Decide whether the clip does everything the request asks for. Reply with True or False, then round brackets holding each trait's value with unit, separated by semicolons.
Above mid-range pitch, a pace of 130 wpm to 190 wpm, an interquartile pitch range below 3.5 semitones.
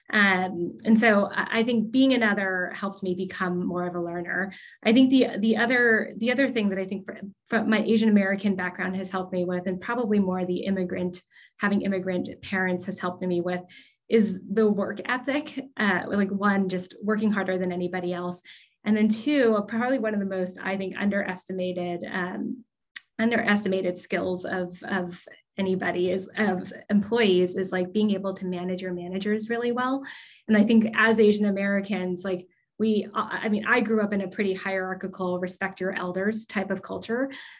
True (195 Hz; 180 wpm; 2.9 semitones)